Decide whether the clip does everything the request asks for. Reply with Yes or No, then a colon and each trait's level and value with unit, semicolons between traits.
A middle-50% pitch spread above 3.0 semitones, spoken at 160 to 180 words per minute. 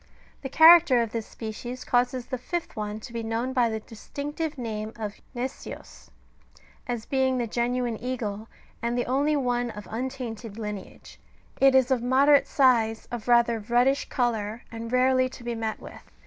No: narrow, 2.5 semitones; average, 170 wpm